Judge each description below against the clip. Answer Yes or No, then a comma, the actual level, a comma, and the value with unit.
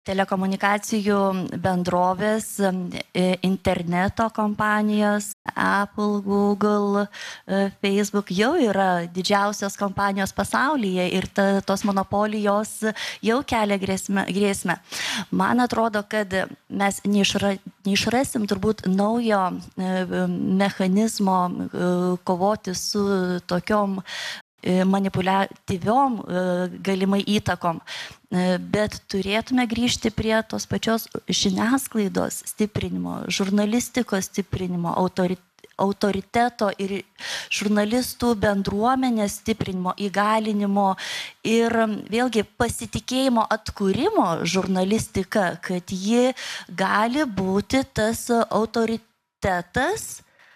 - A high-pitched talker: Yes, high, 200 Hz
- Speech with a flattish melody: Yes, narrow, 2.2 semitones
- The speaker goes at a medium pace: No, slow, 70 wpm